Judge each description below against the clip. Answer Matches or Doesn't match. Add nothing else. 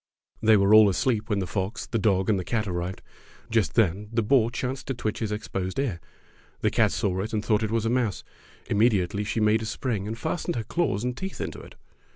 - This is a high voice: Doesn't match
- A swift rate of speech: Matches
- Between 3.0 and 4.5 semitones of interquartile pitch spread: Doesn't match